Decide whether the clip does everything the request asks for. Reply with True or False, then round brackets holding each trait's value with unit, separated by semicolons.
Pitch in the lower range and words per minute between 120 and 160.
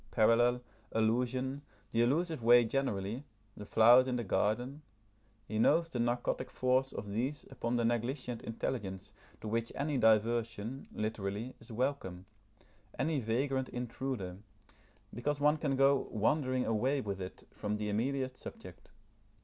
True (120 Hz; 135 wpm)